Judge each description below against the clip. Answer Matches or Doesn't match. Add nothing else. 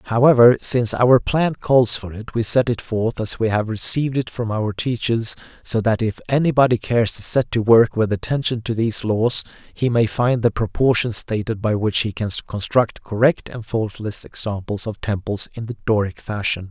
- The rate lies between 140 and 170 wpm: Doesn't match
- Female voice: Doesn't match